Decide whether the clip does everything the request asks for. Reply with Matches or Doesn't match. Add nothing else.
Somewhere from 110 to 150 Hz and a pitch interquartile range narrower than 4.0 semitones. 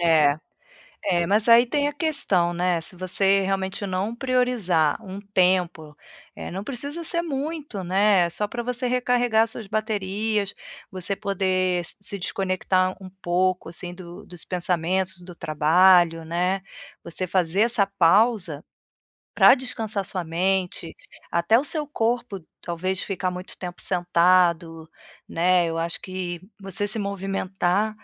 Doesn't match